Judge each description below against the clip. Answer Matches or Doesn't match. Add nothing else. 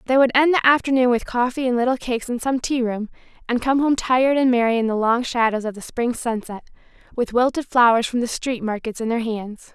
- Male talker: Doesn't match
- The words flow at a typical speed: Doesn't match